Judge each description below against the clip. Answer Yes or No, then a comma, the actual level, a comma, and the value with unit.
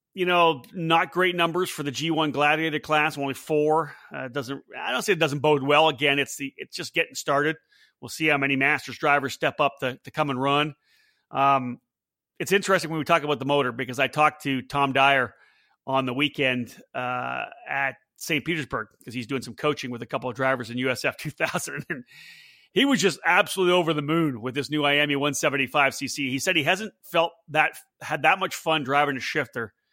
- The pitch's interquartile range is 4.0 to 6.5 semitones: No, average, 3.0 semitones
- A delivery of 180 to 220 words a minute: Yes, fast, 205 wpm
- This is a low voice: No, medium, 145 Hz